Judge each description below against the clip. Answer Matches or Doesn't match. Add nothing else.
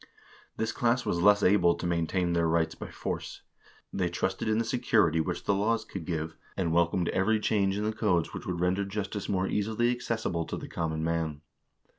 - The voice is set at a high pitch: Doesn't match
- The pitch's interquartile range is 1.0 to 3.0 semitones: Doesn't match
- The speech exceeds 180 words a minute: Matches